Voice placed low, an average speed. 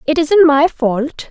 No: very high, 295 Hz; average, 185 wpm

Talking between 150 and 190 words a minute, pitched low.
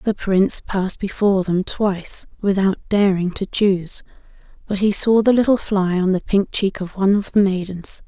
No: average, 185 wpm; high, 195 Hz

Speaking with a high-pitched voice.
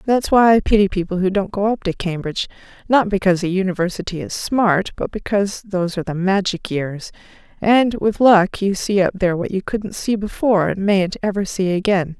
Yes: high, 195 Hz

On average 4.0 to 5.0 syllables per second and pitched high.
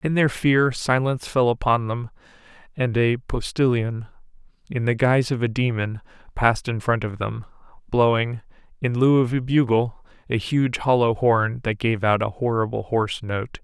No: 4.8 syllables/s; low, 120 Hz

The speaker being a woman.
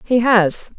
Yes: female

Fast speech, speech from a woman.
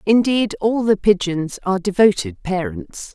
No: slow, 135 wpm; female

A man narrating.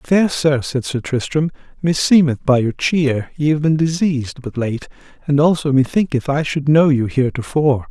Yes: male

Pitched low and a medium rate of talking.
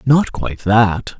Yes: low, 110 Hz; average, 150 wpm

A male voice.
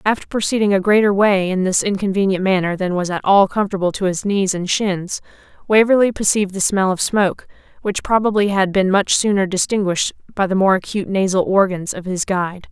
No: female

